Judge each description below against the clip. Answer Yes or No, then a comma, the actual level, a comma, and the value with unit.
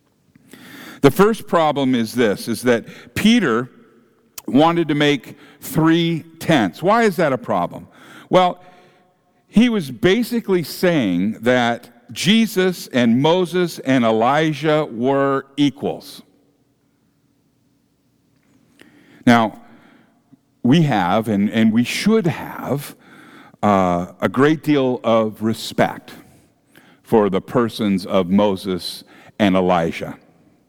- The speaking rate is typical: No, slow, 100 wpm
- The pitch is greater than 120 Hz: Yes, medium, 140 Hz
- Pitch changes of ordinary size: No, wide, 8.0 semitones